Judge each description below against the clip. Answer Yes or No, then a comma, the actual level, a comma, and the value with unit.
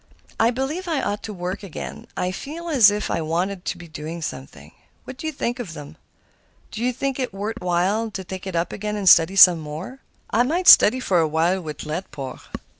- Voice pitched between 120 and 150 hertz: No, high, 195 Hz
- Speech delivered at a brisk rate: Yes, fast, 215 wpm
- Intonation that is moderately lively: No, wide, 6.3 semitones